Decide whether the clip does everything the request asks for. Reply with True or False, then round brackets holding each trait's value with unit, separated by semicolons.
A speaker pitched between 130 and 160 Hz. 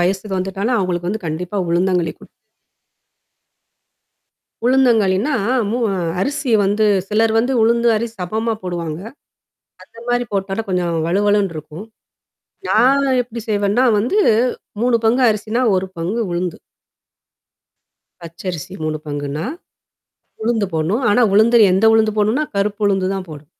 False (205 Hz)